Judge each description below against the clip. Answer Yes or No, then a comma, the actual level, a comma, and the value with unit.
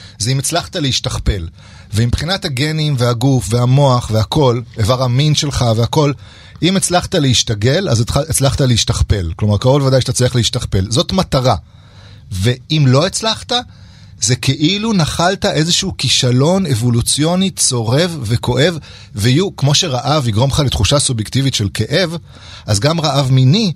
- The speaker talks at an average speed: Yes, average, 130 wpm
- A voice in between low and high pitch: No, low, 130 Hz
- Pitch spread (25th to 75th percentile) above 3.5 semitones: Yes, average, 4.9 semitones